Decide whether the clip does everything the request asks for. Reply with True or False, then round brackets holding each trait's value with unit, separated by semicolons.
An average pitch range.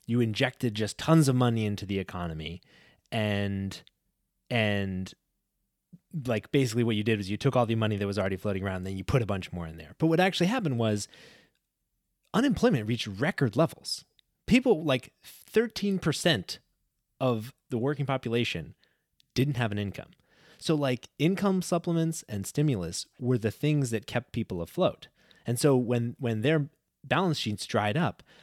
False (5.9 semitones)